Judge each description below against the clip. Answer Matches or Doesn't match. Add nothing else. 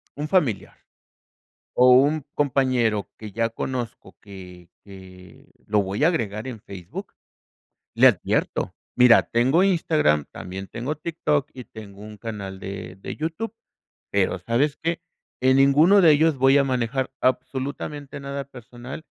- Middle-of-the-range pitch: Doesn't match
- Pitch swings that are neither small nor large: Doesn't match